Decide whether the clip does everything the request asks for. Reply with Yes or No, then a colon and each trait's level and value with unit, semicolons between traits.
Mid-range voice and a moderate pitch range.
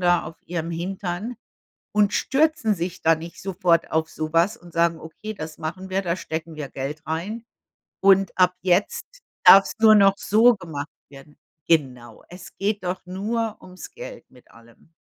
Yes: medium, 180 Hz; average, 4.0 semitones